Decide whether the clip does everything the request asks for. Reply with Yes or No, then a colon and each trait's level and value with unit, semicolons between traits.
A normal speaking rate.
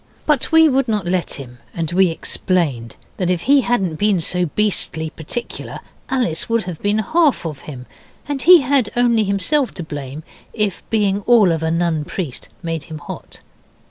Yes: average, 175 wpm